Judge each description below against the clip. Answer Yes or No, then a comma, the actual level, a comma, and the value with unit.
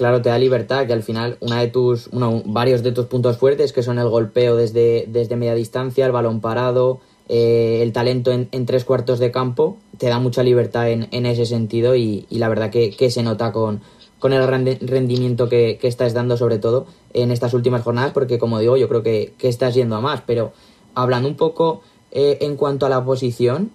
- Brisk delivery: Yes, fast, 220 wpm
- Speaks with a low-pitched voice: Yes, low, 125 Hz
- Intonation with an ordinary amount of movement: No, narrow, 1.6 semitones